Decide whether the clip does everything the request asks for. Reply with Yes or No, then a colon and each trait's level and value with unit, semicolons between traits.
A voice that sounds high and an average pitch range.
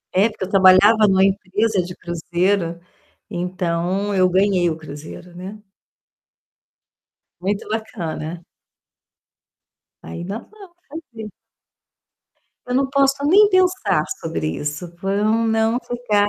Yes: high, 195 Hz; average, 4.2 semitones